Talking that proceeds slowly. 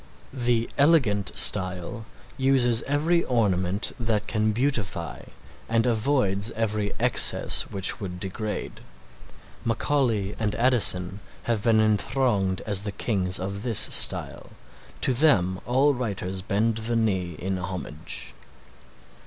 Yes: slow, 115 wpm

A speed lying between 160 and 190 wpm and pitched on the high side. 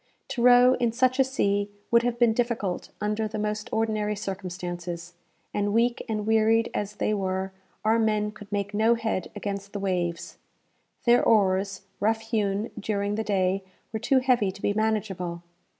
Yes: average, 165 wpm; high, 210 Hz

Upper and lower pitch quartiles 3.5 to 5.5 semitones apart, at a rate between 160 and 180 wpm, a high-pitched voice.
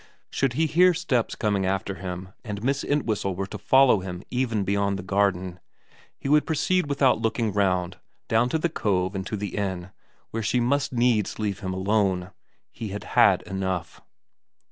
No: average, 4.7 semitones; average, 175 wpm; low, 105 Hz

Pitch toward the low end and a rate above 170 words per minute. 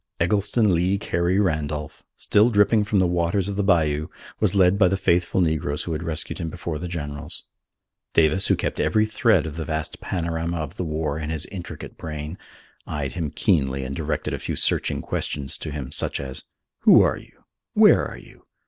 Yes: very low, 85 Hz; average, 195 wpm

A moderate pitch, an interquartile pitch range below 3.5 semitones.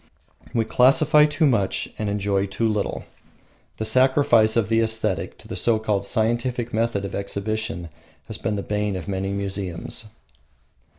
No: low, 110 Hz; average, 2.8 semitones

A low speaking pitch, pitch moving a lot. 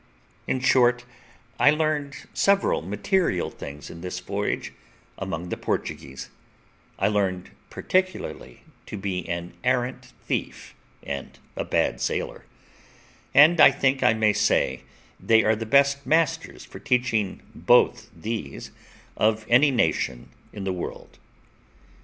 Yes: low, 110 Hz; wide, 7.1 semitones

